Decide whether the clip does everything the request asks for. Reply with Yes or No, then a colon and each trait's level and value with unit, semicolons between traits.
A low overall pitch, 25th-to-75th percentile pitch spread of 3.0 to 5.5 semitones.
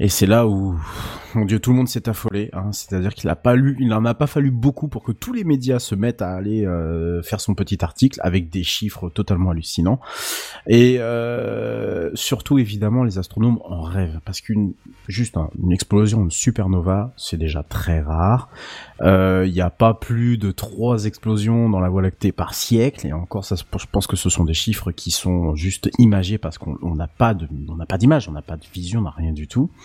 Yes: low, 100 Hz; average, 4.5 semitones